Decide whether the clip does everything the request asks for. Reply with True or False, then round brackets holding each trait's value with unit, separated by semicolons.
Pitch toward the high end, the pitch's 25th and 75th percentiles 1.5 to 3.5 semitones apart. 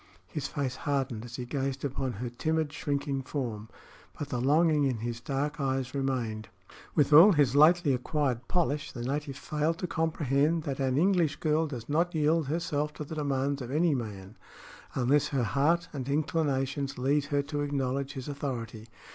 False (140 Hz; 2.6 semitones)